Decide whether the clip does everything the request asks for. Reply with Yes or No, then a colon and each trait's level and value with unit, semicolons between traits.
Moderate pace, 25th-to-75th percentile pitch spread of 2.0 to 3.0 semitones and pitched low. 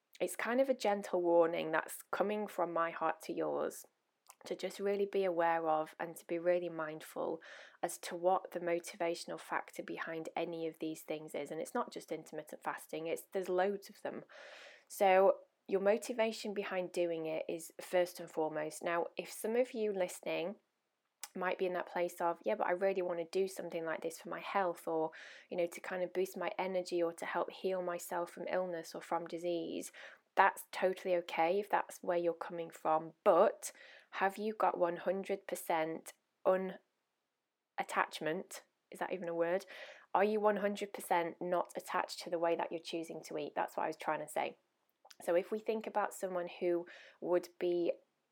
No: average, 185 wpm; narrow, 2.5 semitones; medium, 180 Hz